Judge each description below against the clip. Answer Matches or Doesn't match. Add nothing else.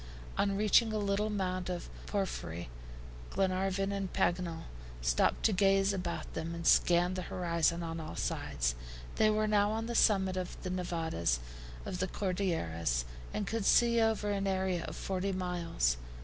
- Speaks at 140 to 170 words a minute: Matches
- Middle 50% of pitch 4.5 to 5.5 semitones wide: Doesn't match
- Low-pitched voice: Doesn't match